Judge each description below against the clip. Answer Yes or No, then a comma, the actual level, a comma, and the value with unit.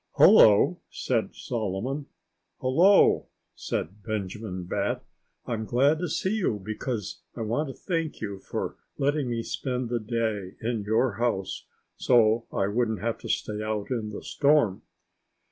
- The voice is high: No, low, 115 Hz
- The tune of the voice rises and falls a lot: No, average, 3.6 semitones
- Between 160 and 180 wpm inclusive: No, average, 145 wpm